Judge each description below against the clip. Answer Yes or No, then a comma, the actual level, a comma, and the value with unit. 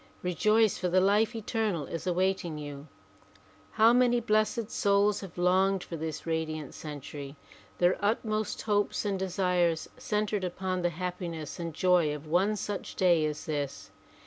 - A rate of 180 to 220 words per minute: No, average, 145 wpm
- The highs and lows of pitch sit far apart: No, average, 4.3 semitones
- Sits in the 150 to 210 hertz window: Yes, medium, 185 Hz